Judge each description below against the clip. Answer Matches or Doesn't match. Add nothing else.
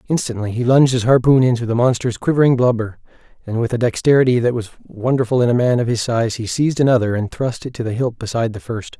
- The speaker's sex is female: Doesn't match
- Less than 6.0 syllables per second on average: Doesn't match